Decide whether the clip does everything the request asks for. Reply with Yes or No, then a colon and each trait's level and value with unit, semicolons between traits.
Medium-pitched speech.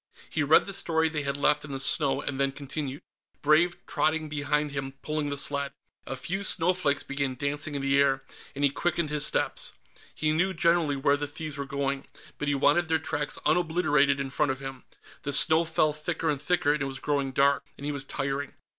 Yes: medium, 145 Hz